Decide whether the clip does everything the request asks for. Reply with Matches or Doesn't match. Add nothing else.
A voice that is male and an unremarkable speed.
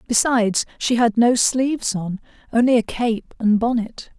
Doesn't match